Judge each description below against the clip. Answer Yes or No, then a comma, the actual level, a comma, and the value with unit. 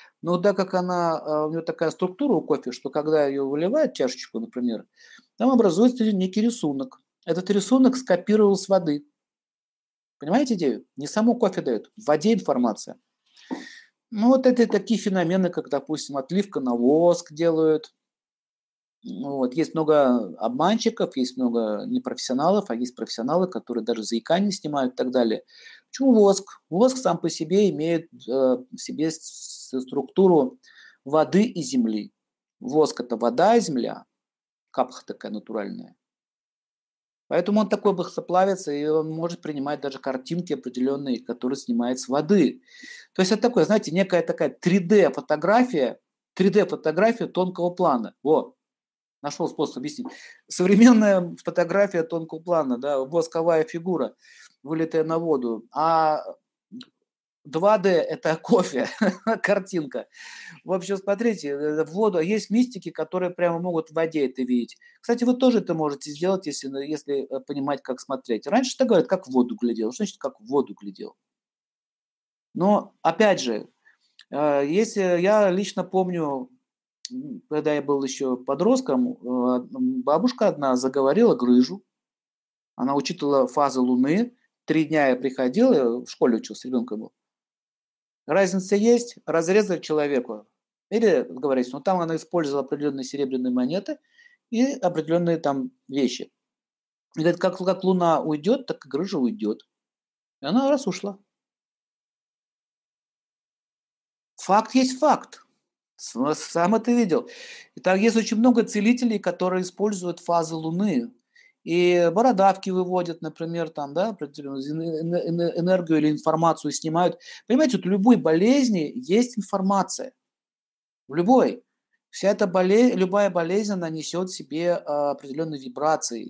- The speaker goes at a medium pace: Yes, average, 130 wpm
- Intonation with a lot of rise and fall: Yes, wide, 6.6 semitones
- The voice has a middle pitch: Yes, medium, 175 Hz